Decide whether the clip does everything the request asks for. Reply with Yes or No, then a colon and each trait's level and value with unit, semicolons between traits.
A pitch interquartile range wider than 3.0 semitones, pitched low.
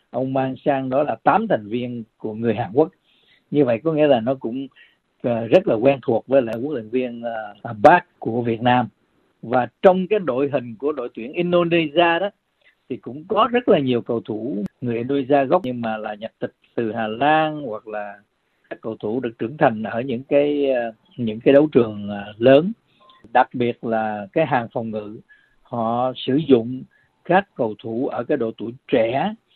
Yes: average, 4.5 semitones; low, 130 Hz